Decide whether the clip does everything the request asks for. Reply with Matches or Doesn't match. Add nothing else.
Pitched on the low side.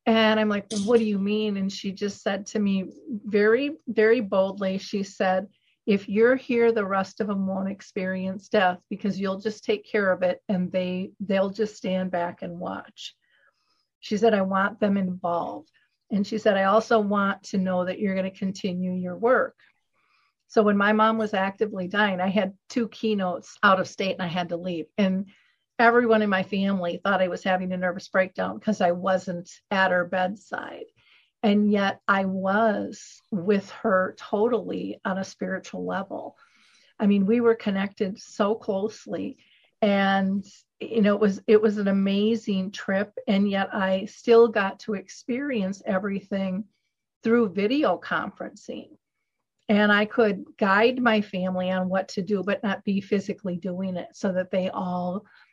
Doesn't match